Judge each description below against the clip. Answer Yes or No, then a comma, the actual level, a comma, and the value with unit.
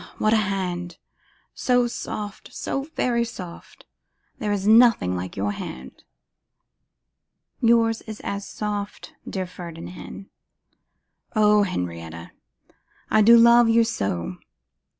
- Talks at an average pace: No, slow, 110 wpm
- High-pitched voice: Yes, high, 205 Hz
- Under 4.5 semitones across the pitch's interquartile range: No, average, 4.9 semitones